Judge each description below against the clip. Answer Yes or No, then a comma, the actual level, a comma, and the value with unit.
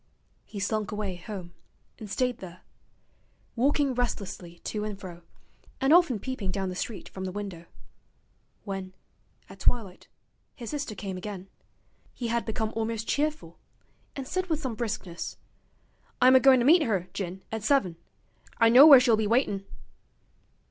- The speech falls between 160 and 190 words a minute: No, average, 150 wpm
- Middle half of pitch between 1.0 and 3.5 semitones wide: No, average, 4.8 semitones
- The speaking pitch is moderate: No, high, 215 Hz